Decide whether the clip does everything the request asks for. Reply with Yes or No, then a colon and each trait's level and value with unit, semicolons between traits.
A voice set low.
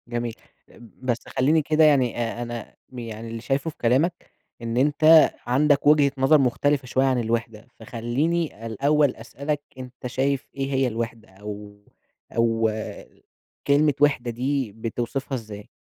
Yes: low, 125 Hz